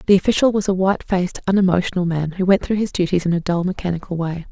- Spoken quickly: Yes, fast, 240 wpm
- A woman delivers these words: Yes, female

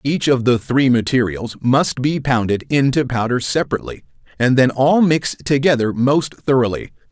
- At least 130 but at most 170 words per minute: Yes, average, 150 wpm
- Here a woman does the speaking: No, male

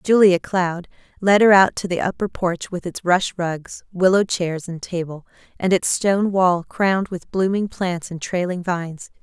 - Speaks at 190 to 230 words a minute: No, average, 180 wpm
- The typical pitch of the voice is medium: Yes, medium, 180 Hz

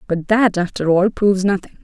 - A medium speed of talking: Yes, average, 195 wpm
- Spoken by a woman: Yes, female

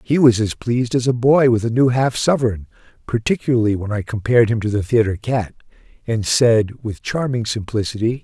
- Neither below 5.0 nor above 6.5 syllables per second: Yes, 5.5 syllables/s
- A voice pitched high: No, low, 115 Hz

